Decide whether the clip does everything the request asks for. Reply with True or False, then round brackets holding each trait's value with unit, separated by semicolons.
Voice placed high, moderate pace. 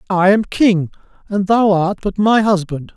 True (195 Hz; 180 wpm)